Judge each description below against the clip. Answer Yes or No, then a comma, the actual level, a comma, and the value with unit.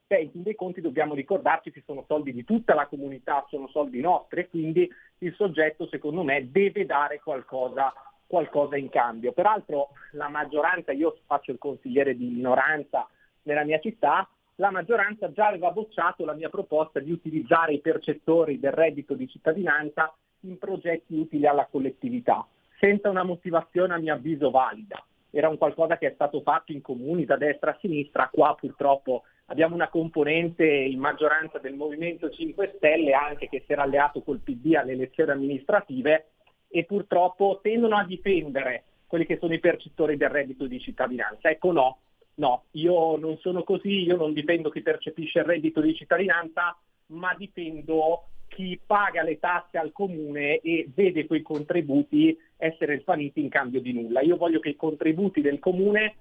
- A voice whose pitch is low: No, medium, 160 Hz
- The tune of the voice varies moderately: Yes, average, 3.3 semitones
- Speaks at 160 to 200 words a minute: Yes, fast, 170 wpm